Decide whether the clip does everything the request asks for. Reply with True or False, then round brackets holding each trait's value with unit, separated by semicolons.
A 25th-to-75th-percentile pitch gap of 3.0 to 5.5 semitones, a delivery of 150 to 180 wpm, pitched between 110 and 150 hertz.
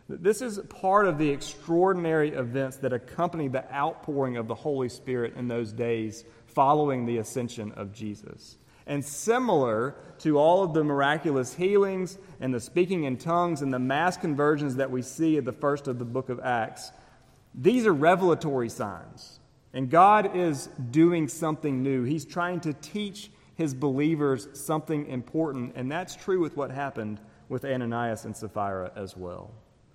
True (4.7 semitones; 160 wpm; 140 Hz)